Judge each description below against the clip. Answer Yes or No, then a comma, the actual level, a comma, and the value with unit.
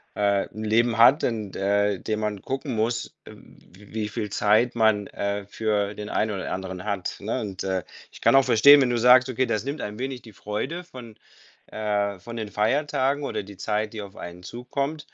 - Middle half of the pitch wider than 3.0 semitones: Yes, average, 3.4 semitones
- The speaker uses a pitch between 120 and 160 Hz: No, low, 110 Hz